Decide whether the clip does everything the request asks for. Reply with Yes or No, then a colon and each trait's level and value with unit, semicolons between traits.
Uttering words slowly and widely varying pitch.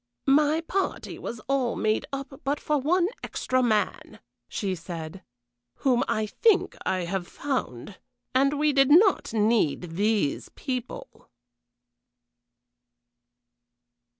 Yes: slow, 110 wpm; wide, 6.3 semitones